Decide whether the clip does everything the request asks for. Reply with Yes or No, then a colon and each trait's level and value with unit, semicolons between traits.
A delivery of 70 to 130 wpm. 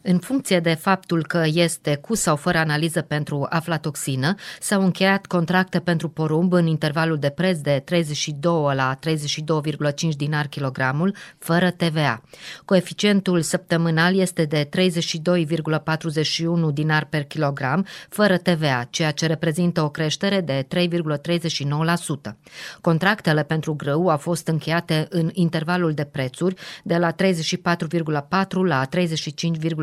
Yes: average, 125 wpm